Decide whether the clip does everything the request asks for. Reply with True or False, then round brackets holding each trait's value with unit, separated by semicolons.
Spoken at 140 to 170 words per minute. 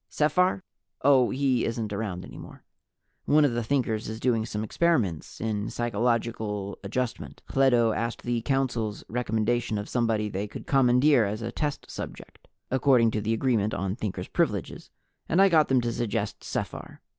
True (160 wpm)